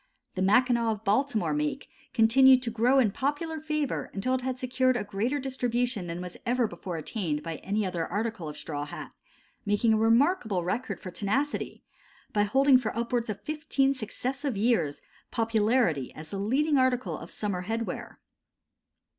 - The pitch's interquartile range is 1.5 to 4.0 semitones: No, average, 4.7 semitones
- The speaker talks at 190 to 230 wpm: No, average, 165 wpm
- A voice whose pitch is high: Yes, high, 230 Hz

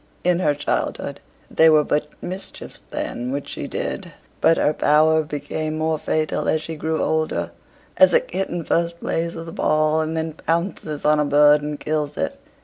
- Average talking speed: Yes, average, 180 wpm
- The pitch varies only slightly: Yes, narrow, 1.6 semitones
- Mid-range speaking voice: Yes, medium, 155 Hz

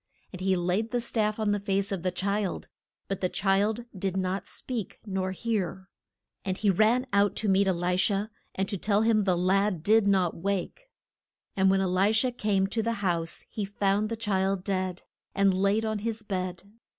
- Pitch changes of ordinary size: No, narrow, 2.2 semitones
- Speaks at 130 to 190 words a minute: No, average, 200 wpm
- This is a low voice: No, high, 195 Hz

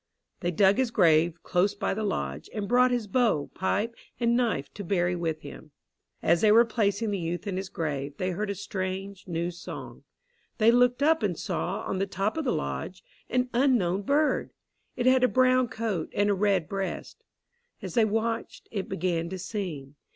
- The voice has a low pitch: No, high, 200 Hz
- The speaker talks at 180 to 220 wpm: Yes, average, 190 wpm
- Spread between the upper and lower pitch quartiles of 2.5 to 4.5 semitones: No, average, 4.9 semitones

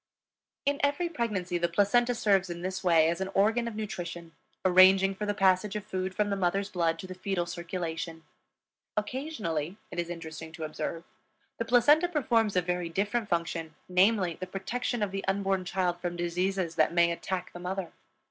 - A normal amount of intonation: Yes, average, 3.2 semitones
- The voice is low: No, medium, 185 Hz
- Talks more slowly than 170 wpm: No, average, 180 wpm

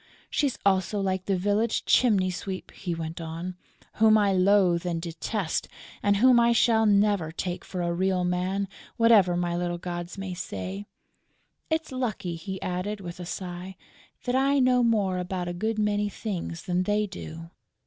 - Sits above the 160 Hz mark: Yes, high, 190 Hz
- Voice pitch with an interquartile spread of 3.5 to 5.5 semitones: No, average, 3.1 semitones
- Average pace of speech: Yes, average, 170 wpm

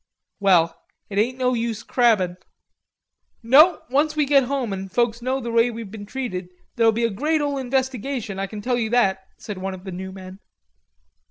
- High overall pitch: Yes, high, 230 Hz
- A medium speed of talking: Yes, average, 190 wpm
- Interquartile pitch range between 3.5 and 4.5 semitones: No, average, 4.9 semitones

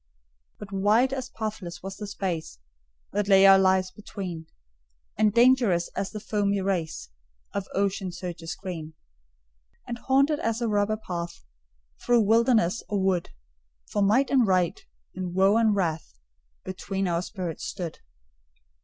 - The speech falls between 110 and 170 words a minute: Yes, average, 140 wpm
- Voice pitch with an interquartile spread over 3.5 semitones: No, average, 3.1 semitones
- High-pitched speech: Yes, high, 195 Hz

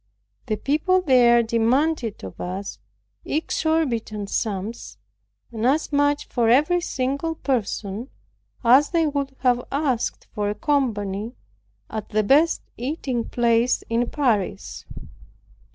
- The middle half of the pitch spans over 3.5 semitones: Yes, average, 4.6 semitones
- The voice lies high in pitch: Yes, high, 245 Hz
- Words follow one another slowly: Yes, slow, 115 wpm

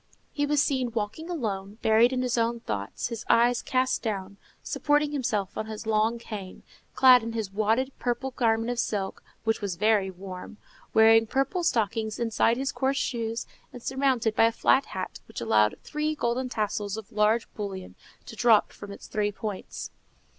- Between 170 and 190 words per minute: Yes, average, 175 wpm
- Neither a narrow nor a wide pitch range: Yes, average, 3.3 semitones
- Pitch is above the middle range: Yes, high, 225 Hz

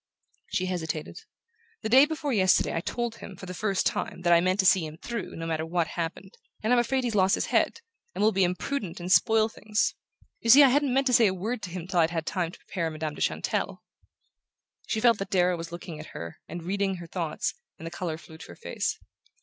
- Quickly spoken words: Yes, fast, 240 wpm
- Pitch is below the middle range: No, medium, 185 Hz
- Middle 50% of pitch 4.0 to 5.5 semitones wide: Yes, average, 4.7 semitones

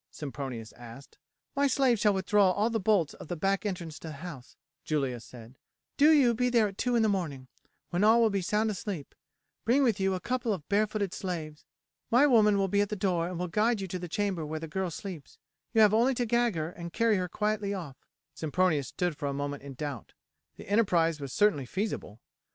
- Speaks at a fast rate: Yes, fast, 220 wpm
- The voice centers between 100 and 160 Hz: No, high, 190 Hz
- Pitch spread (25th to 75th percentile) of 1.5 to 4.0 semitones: No, wide, 5.6 semitones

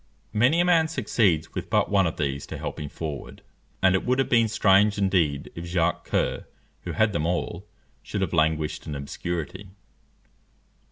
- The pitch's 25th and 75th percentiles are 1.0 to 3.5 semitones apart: No, average, 5.2 semitones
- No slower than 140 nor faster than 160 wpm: No, average, 175 wpm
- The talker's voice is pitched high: No, very low, 95 Hz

